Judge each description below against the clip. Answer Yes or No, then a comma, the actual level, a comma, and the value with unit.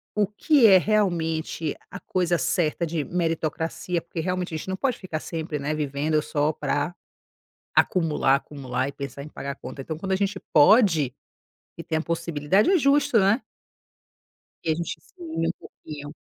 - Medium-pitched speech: Yes, medium, 165 Hz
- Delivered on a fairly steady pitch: No, average, 3.7 semitones